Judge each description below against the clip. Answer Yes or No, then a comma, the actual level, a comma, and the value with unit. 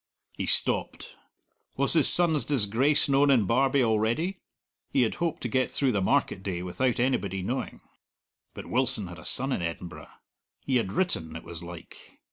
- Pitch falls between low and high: No, low, 125 Hz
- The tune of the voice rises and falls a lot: Yes, wide, 6.3 semitones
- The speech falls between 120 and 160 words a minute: No, average, 170 wpm